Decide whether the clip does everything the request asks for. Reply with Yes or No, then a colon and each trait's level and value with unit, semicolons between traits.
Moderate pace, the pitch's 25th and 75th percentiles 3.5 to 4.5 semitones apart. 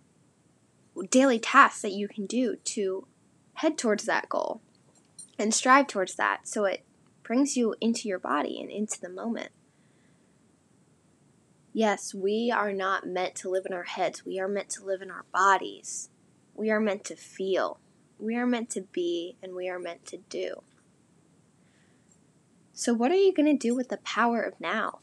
Yes: average, 175 wpm; average, 3.8 semitones